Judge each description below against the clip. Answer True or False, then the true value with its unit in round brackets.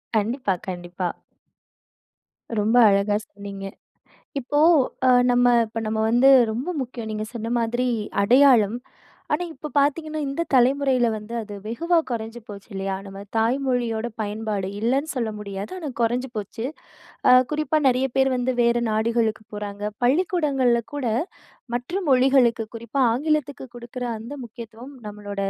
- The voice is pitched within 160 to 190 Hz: False (235 Hz)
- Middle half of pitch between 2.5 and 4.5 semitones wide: True (3.7 semitones)